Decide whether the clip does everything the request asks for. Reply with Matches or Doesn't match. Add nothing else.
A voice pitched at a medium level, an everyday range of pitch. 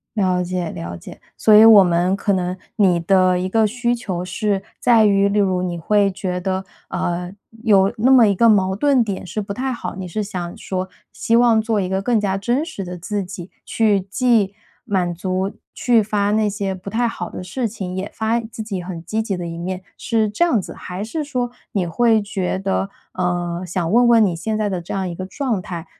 Doesn't match